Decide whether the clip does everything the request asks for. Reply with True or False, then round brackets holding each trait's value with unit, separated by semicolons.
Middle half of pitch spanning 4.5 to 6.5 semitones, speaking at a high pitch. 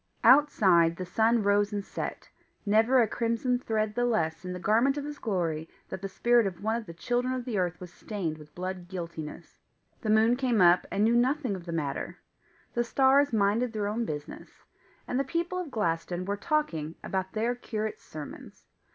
True (5.1 semitones; 215 Hz)